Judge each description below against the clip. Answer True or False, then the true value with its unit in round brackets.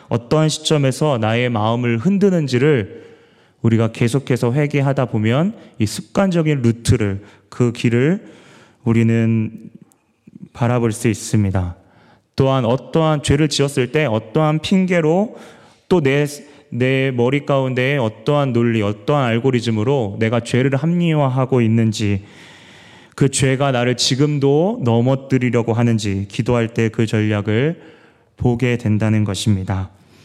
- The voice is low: True (125 Hz)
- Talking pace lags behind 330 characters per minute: True (275 characters per minute)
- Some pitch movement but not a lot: True (4.2 semitones)